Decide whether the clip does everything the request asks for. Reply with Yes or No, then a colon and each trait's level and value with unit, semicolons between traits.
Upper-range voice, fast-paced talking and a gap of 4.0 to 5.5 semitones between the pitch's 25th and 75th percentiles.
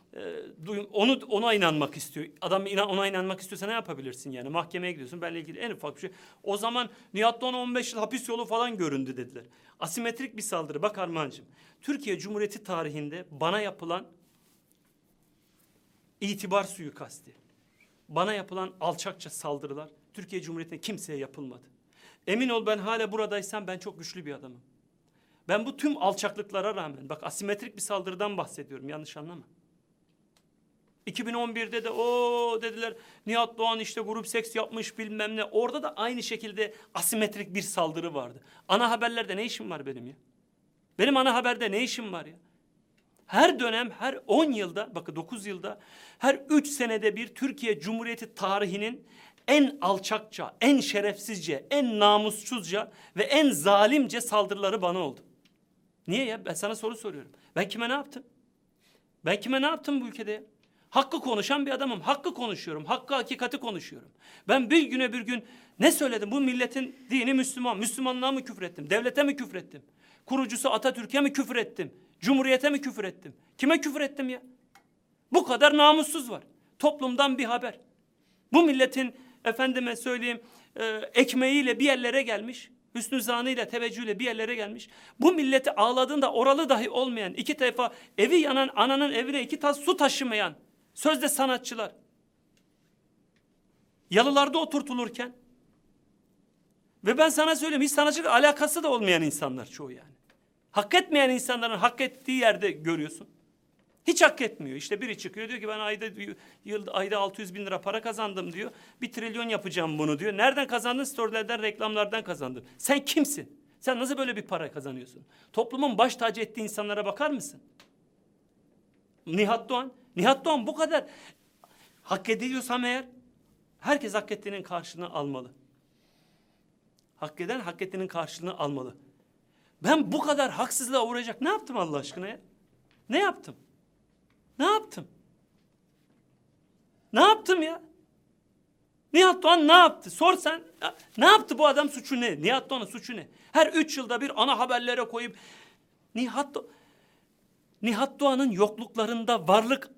Yes: high, 230 Hz; fast, 145 wpm; average, 5.2 semitones